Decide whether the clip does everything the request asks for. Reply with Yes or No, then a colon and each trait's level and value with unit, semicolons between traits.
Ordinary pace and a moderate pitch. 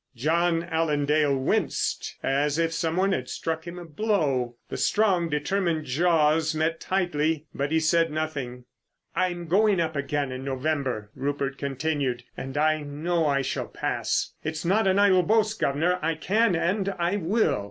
Yes: average, 165 wpm; medium, 160 Hz